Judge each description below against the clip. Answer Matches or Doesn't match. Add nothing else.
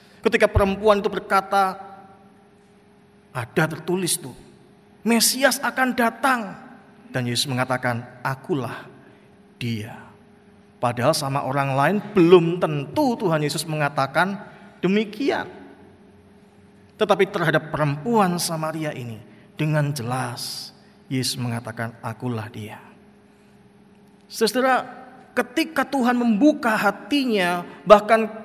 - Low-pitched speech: Doesn't match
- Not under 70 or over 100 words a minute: Matches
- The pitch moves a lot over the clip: Matches